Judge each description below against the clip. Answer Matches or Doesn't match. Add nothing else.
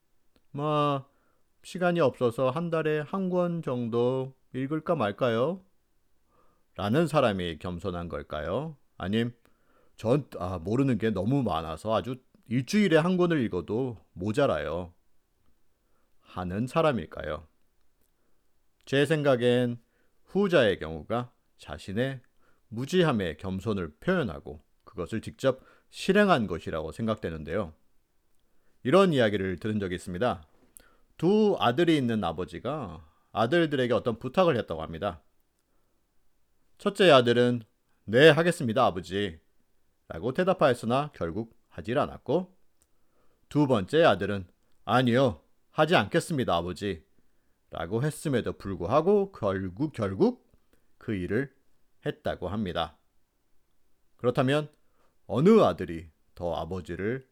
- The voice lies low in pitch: Matches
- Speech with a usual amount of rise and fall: Doesn't match